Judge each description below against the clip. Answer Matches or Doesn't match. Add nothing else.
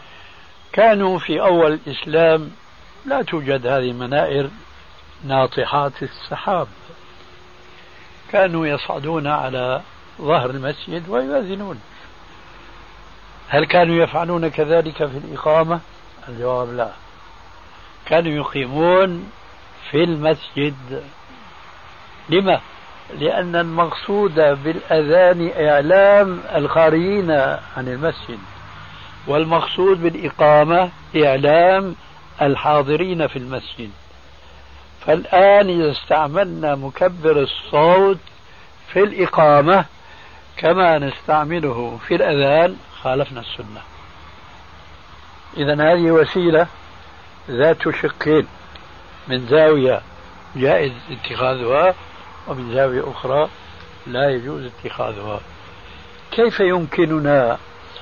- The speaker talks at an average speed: Matches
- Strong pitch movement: Matches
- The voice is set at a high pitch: Doesn't match